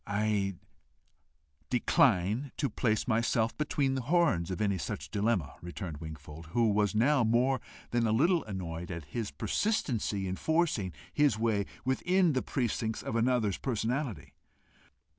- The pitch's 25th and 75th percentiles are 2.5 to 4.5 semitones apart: No, average, 5.2 semitones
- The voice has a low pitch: Yes, low, 110 Hz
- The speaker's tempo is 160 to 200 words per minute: No, average, 140 wpm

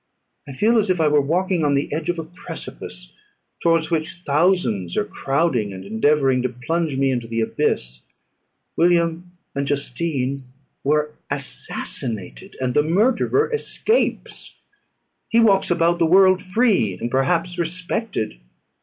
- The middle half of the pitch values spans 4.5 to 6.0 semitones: Yes, wide, 5.6 semitones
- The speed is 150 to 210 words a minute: No, average, 140 wpm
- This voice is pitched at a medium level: Yes, medium, 155 Hz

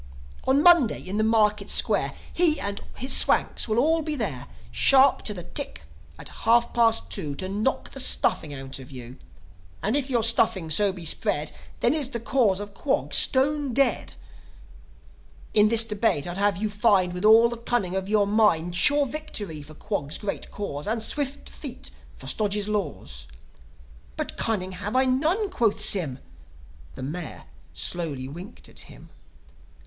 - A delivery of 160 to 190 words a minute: Yes, average, 165 wpm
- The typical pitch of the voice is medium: No, high, 210 Hz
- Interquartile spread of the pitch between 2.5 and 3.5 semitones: No, wide, 5.5 semitones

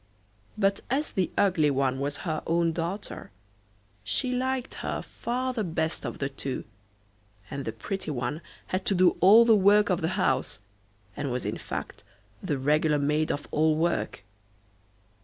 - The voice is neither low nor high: Yes, medium, 165 Hz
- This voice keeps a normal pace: Yes, average, 160 wpm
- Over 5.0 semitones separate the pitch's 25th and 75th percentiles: Yes, wide, 5.5 semitones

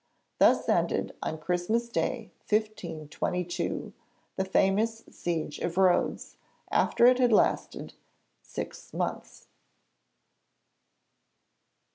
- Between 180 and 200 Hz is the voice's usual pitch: Yes, high, 190 Hz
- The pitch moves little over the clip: No, average, 4.5 semitones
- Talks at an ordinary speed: No, slow, 85 wpm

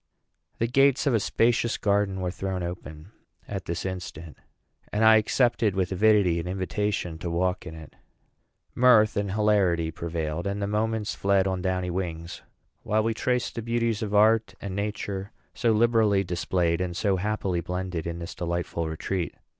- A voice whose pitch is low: Yes, very low, 95 Hz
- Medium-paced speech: Yes, average, 165 wpm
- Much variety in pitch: No, average, 3.5 semitones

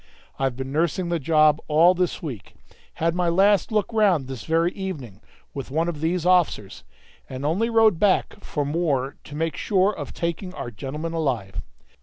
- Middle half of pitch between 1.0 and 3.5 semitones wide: No, average, 4.7 semitones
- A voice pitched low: No, medium, 165 Hz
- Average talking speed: Yes, average, 175 wpm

